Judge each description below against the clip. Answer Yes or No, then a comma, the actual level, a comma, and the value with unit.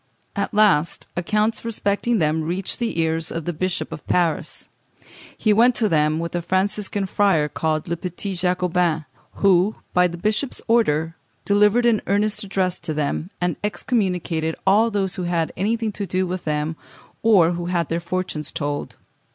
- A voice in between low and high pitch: Yes, medium, 180 Hz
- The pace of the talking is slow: No, average, 165 wpm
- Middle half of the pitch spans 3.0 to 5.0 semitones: Yes, average, 3.9 semitones